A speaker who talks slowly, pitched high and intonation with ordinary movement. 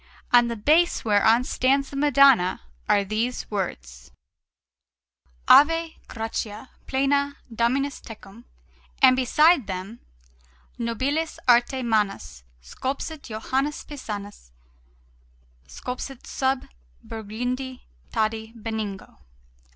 Yes: slow, 90 wpm; high, 240 Hz; average, 4.2 semitones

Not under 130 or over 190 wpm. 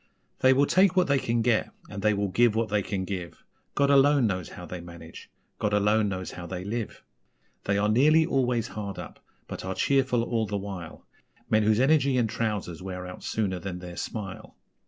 No: average, 200 wpm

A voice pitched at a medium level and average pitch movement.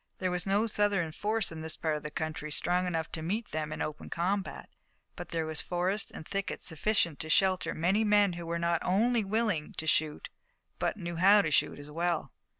Yes: medium, 175 Hz; average, 4.1 semitones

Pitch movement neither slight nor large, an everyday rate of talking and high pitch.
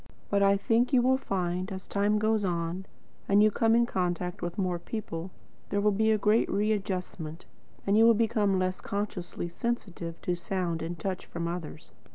Yes: average, 3.4 semitones; average, 185 wpm; high, 195 Hz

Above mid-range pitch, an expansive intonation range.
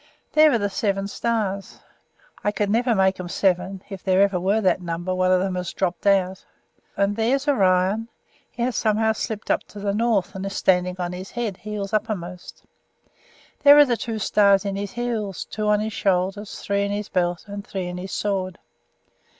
No: high, 200 Hz; narrow, 2.5 semitones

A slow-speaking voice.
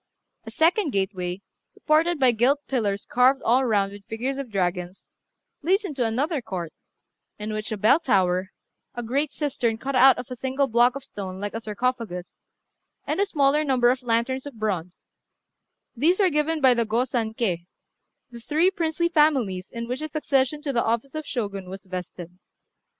No: average, 180 wpm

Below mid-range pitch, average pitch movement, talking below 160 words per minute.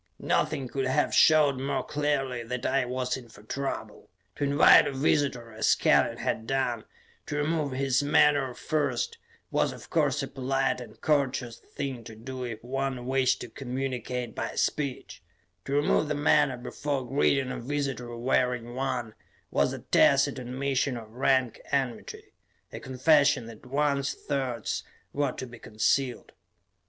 No: low, 130 Hz; narrow, 2.3 semitones; average, 150 wpm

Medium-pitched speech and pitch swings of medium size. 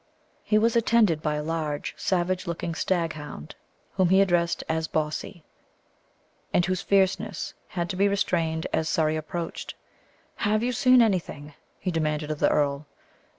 Yes: medium, 170 Hz; average, 3.8 semitones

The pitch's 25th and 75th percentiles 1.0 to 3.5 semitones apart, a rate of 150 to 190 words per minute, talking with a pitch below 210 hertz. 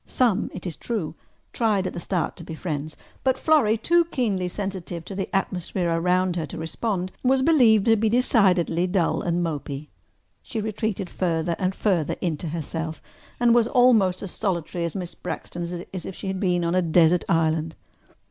No: average, 4.2 semitones; average, 180 wpm; medium, 185 Hz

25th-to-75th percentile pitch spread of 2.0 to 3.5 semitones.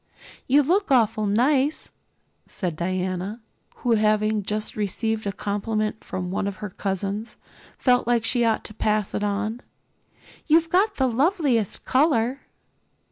No: average, 3.9 semitones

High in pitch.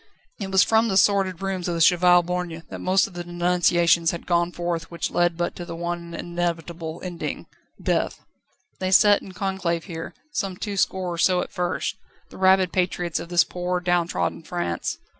No: medium, 175 Hz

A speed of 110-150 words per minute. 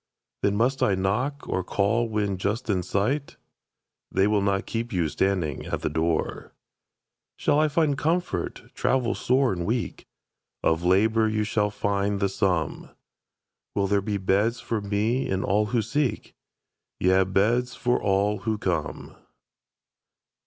Yes: average, 145 wpm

